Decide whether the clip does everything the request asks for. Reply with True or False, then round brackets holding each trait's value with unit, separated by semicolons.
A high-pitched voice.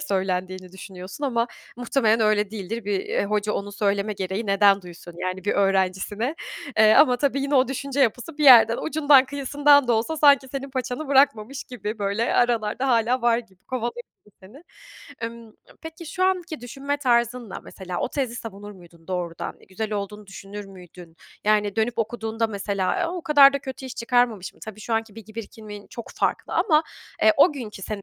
True (225 Hz)